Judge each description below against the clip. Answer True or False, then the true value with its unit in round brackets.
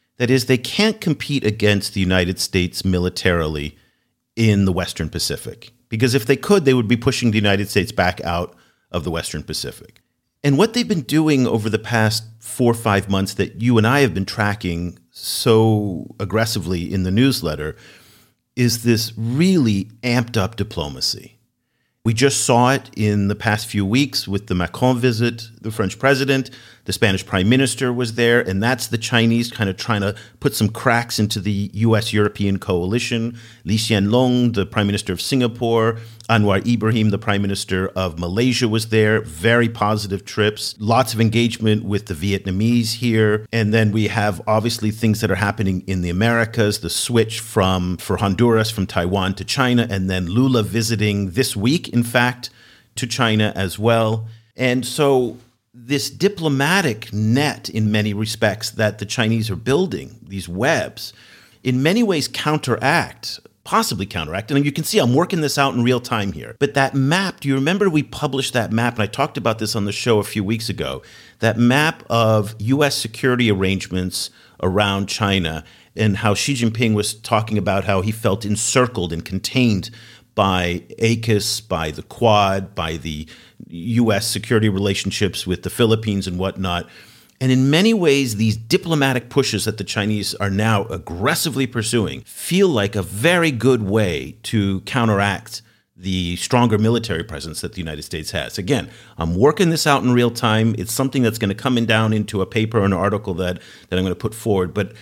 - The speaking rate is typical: True (175 wpm)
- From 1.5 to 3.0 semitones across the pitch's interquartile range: False (3.6 semitones)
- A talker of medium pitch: False (110 Hz)